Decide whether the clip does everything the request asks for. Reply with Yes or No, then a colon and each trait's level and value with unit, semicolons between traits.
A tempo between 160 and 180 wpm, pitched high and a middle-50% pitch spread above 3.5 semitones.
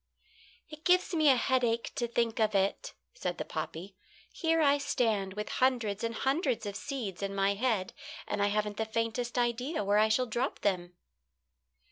Yes: average, 175 wpm; high, 230 Hz; average, 4.2 semitones